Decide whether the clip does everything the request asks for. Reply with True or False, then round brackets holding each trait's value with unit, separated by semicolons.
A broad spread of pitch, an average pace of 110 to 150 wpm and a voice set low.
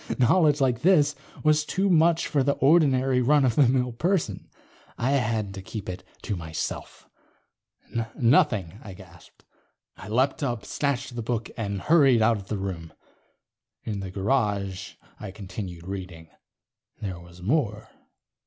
True (6.4 semitones; 145 wpm; 115 Hz)